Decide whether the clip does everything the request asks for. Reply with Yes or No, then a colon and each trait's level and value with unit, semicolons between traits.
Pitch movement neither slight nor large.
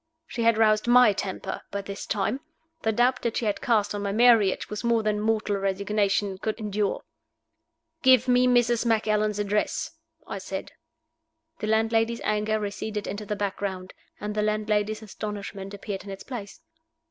No: narrow, 1.9 semitones